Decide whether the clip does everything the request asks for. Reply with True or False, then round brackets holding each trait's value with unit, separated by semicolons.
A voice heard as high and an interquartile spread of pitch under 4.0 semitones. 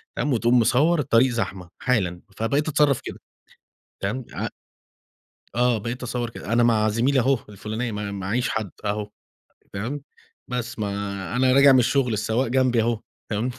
False (120 Hz; 3.1 semitones)